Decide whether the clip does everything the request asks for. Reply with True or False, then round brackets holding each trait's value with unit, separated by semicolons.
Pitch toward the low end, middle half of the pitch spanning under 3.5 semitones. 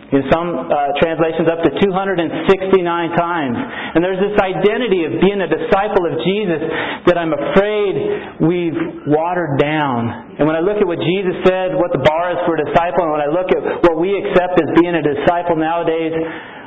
False (175 Hz; 2.8 semitones)